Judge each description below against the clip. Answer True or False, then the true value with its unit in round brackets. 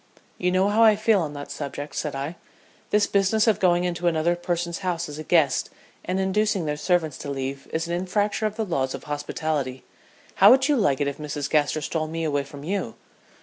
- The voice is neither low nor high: True (170 Hz)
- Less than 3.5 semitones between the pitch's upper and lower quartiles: False (4.7 semitones)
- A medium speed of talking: False (215 wpm)